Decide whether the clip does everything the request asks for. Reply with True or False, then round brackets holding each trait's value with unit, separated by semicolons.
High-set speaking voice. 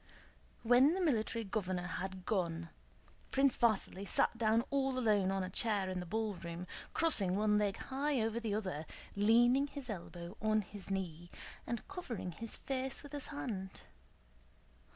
True (215 Hz)